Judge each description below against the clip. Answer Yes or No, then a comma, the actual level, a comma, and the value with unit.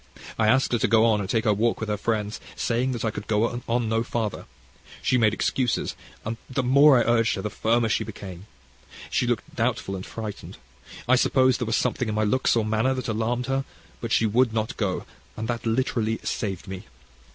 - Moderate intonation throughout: No, narrow, 2.2 semitones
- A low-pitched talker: Yes, low, 115 Hz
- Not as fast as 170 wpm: No, fast, 205 wpm